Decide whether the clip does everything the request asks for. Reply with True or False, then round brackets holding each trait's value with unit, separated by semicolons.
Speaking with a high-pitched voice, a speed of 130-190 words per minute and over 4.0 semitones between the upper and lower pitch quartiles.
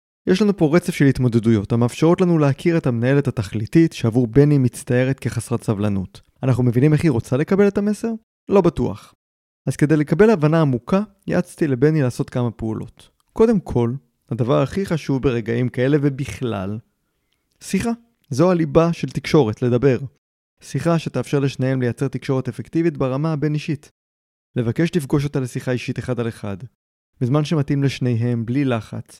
False (135 Hz; 150 wpm; 5.1 semitones)